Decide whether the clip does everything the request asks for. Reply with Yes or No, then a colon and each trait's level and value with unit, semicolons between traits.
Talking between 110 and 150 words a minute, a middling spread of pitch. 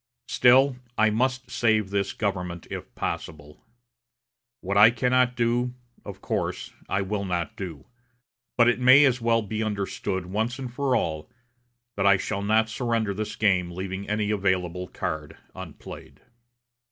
Yes: average, 140 wpm; average, 4.0 semitones